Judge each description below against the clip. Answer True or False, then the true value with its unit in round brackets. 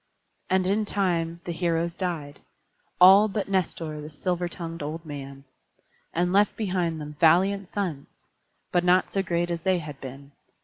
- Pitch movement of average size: True (3.1 semitones)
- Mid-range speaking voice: True (175 Hz)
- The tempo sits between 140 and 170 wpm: True (160 wpm)